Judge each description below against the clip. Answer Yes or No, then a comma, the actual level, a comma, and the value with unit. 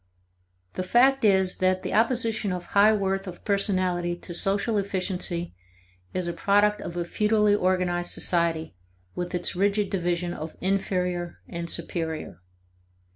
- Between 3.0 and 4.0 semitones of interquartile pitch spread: No, narrow, 2.5 semitones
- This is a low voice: No, medium, 185 Hz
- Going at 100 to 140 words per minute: Yes, slow, 135 wpm